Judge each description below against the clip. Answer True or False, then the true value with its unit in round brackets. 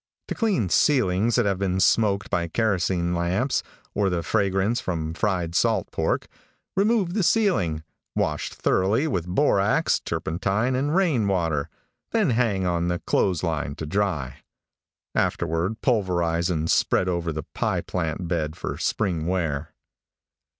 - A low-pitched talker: True (95 Hz)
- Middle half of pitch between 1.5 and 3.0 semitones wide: False (4.9 semitones)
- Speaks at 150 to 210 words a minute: False (140 wpm)